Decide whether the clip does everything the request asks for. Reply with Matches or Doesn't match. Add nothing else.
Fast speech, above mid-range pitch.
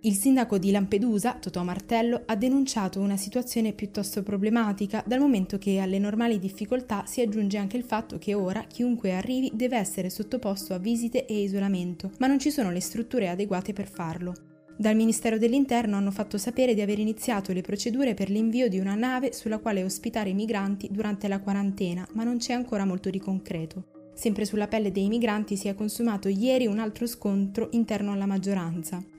Matches